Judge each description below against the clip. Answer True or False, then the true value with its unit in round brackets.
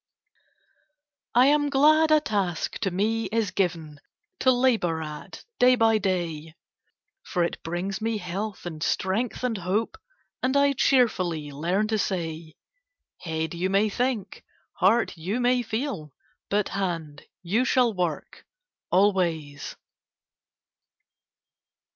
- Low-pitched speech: False (195 Hz)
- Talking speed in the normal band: False (120 wpm)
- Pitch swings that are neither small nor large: False (5.8 semitones)